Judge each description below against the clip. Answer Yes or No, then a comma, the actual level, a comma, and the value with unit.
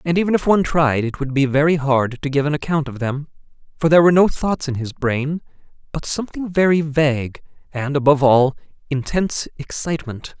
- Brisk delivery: No, average, 190 wpm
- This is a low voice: No, medium, 150 Hz